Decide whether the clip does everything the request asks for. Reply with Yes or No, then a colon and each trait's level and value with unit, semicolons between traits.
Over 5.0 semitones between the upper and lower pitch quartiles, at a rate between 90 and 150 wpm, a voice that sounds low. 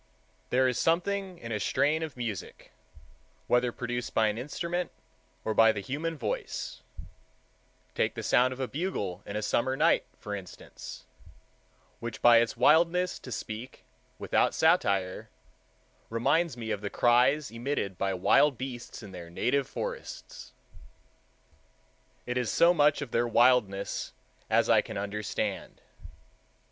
Yes: wide, 5.4 semitones; slow, 135 wpm; low, 120 Hz